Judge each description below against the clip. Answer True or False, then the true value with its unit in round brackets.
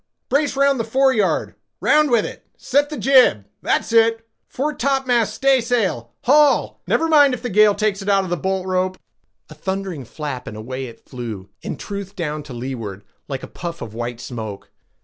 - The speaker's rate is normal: True (155 wpm)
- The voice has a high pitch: True (195 Hz)